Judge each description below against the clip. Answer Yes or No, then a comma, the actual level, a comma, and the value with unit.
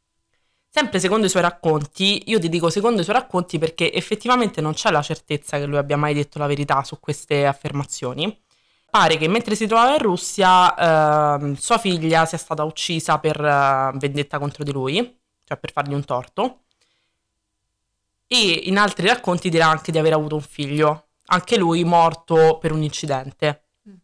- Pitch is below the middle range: No, medium, 160 Hz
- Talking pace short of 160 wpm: No, fast, 170 wpm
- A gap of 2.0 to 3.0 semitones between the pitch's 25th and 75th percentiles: No, average, 4.1 semitones